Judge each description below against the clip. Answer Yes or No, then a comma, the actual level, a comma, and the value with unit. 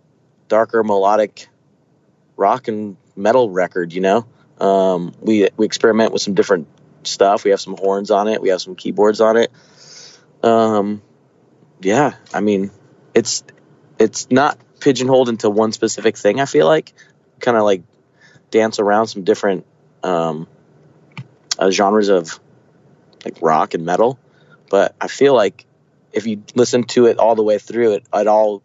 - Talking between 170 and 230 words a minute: No, average, 155 wpm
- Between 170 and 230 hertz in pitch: No, low, 105 Hz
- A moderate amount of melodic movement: No, narrow, 2.3 semitones